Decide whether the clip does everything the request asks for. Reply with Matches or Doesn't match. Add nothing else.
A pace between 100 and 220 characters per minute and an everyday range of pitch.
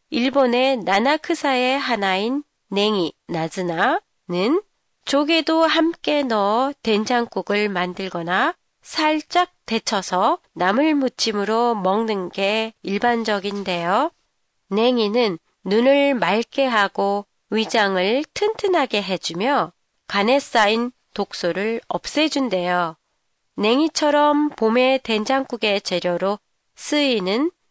Doesn't match